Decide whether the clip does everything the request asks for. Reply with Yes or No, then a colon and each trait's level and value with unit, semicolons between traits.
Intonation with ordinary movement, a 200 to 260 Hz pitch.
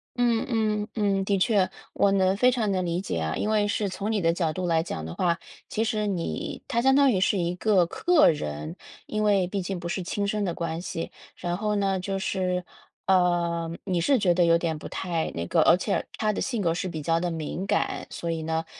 No: average, 3.6 semitones; medium, 185 Hz